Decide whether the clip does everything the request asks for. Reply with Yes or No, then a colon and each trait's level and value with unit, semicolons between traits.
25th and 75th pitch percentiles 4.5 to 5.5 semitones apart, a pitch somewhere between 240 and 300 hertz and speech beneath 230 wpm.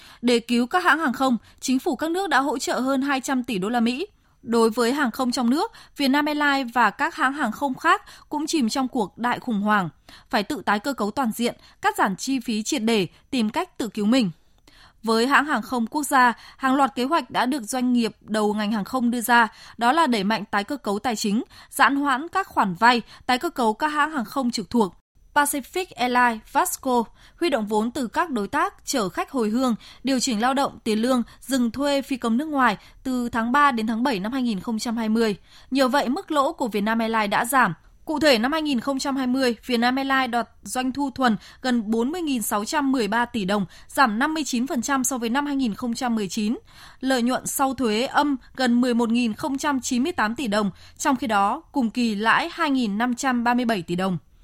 No: average, 3.5 semitones; very high, 250 Hz; average, 200 wpm